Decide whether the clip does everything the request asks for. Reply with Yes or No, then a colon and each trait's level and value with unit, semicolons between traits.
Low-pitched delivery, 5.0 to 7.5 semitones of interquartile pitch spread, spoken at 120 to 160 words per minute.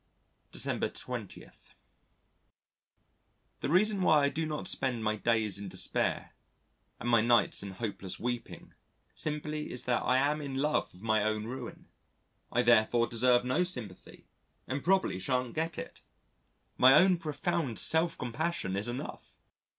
Yes: low, 125 Hz; average, 5.3 semitones; average, 145 wpm